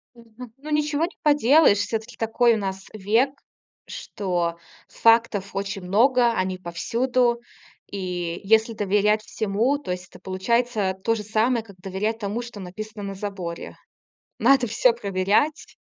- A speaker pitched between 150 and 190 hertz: No, high, 215 Hz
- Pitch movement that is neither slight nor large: Yes, average, 3.7 semitones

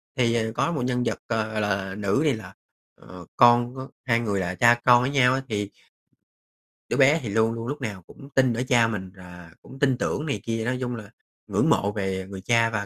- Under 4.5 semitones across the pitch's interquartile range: Yes, average, 3.7 semitones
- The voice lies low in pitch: Yes, low, 115 Hz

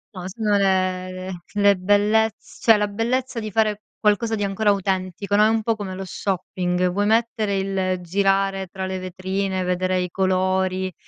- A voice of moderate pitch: No, high, 195 Hz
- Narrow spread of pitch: Yes, narrow, 2.1 semitones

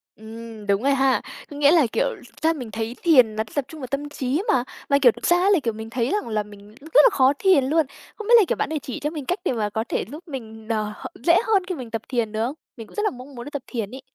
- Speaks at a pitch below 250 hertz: No, very high, 260 Hz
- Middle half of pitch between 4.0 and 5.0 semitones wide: No, wide, 5.6 semitones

